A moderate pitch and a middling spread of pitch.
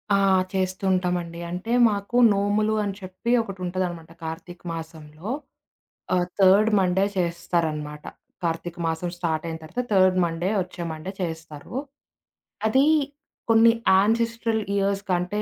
Yes: medium, 180 Hz; average, 3.2 semitones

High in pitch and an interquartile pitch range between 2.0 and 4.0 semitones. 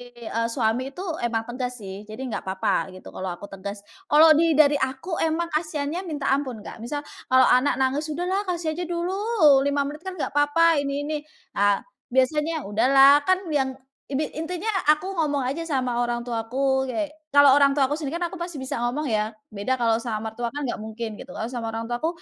No: very high, 275 Hz; average, 4.6 semitones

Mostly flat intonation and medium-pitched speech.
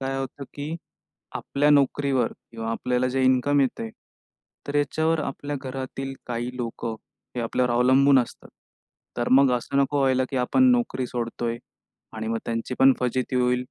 No: narrow, 2.2 semitones; low, 130 Hz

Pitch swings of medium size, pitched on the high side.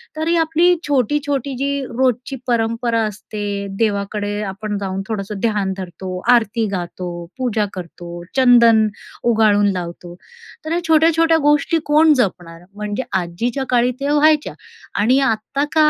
No: wide, 5.8 semitones; high, 225 Hz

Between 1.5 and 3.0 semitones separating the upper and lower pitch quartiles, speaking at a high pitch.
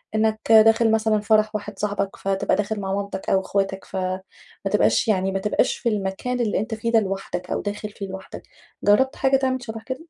Yes: narrow, 2.4 semitones; high, 210 Hz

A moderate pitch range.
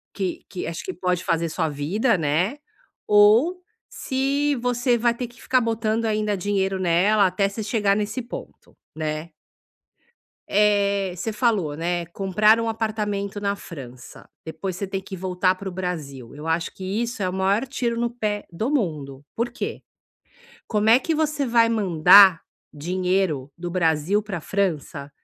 Yes: average, 4.5 semitones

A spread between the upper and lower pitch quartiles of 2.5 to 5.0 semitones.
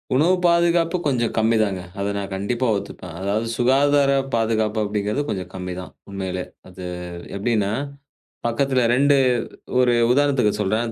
No: wide, 5.4 semitones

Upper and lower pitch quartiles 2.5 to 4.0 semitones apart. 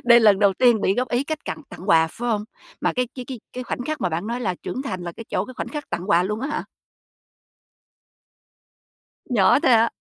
No: average, 4.6 semitones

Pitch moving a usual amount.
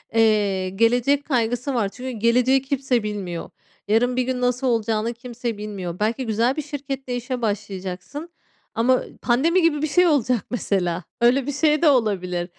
Yes: average, 4.0 semitones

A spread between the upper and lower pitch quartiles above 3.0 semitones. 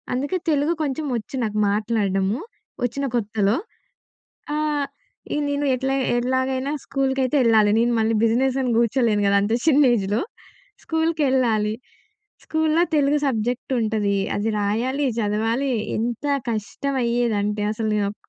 Yes: average, 4.4 semitones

